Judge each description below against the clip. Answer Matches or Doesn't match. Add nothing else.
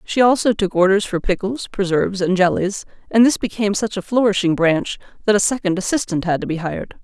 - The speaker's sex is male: Doesn't match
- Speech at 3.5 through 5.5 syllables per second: Doesn't match